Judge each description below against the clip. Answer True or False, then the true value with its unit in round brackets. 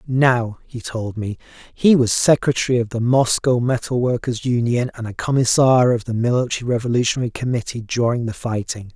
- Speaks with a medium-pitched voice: False (120 Hz)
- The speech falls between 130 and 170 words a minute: True (160 wpm)